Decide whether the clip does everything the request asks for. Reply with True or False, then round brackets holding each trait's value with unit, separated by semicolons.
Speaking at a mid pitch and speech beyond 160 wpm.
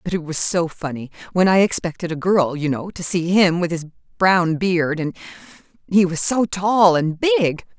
True (175 Hz; 200 wpm)